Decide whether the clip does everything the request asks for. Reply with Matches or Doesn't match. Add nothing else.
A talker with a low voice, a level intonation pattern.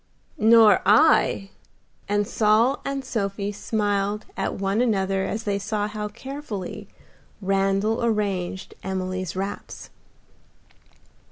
Doesn't match